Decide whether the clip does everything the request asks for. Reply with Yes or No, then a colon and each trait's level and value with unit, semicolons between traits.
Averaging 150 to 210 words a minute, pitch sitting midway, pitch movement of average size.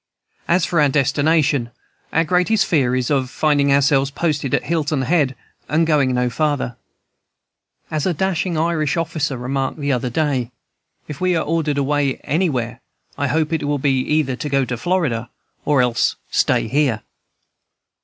Yes: average, 160 wpm; medium, 145 Hz; average, 3.4 semitones